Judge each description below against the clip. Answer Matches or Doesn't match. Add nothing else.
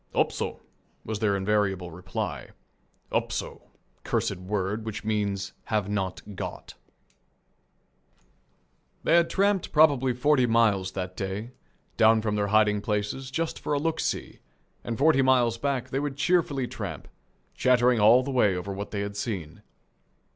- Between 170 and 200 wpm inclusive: Doesn't match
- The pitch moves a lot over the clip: Doesn't match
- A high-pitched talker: Doesn't match